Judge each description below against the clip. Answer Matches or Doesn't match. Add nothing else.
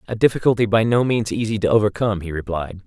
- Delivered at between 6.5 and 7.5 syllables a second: Matches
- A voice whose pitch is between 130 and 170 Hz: Doesn't match